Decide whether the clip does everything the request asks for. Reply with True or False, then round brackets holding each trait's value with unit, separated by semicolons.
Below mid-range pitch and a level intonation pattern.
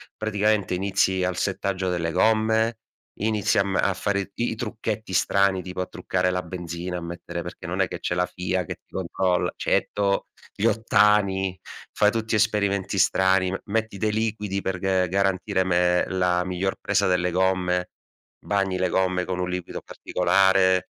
True (95 Hz; 2.0 semitones)